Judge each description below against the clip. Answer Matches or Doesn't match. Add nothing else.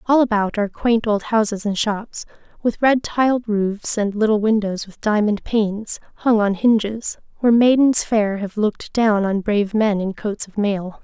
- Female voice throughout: Matches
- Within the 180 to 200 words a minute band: Matches